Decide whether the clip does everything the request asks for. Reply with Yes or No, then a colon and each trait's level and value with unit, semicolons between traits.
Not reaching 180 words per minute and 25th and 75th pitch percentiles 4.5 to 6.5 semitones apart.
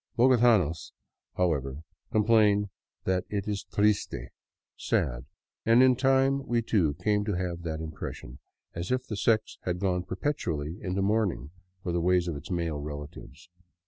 Yes: average, 160 wpm; average, 4.8 semitones